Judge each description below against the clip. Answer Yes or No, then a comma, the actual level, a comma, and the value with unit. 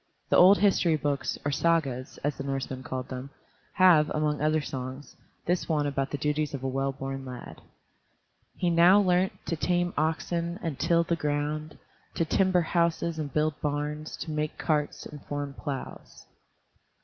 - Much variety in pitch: No, average, 3.3 semitones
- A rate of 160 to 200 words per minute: Yes, average, 165 wpm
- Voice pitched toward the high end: No, medium, 150 Hz